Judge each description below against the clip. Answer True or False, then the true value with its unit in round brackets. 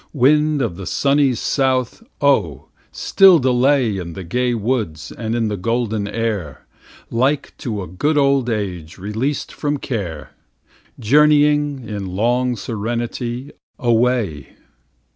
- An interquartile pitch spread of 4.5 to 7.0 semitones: True (5.1 semitones)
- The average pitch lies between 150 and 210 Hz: False (120 Hz)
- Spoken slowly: True (125 wpm)